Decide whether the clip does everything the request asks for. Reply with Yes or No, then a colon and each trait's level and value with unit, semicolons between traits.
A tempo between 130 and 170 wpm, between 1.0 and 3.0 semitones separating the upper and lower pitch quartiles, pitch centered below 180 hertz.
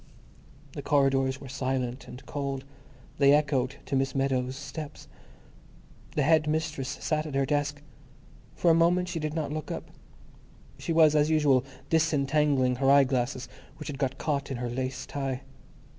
Yes: average, 160 wpm; narrow, 2.4 semitones; medium, 140 Hz